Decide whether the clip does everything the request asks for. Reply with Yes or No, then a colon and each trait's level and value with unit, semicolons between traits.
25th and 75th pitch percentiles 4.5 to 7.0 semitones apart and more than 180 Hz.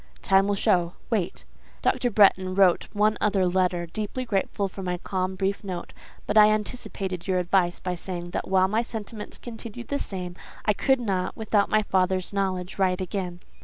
No: narrow, 2.5 semitones; high, 190 Hz